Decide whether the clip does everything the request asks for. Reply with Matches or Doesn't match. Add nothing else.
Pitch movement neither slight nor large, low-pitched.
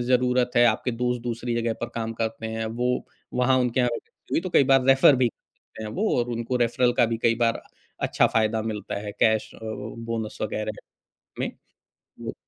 Doesn't match